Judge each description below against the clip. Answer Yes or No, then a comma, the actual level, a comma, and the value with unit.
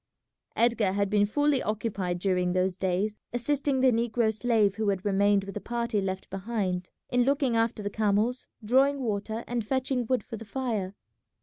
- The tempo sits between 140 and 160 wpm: No, average, 175 wpm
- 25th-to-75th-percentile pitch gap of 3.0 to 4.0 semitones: Yes, average, 3.5 semitones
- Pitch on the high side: Yes, high, 220 Hz